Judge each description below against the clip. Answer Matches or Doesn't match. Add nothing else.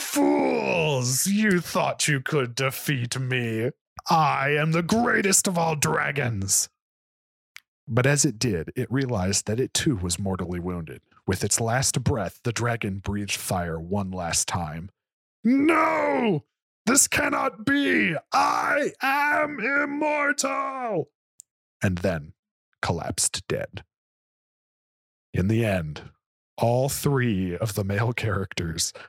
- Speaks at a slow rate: Matches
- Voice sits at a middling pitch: Doesn't match